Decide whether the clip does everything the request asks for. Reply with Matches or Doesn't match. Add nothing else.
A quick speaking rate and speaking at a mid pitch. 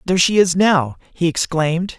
Doesn't match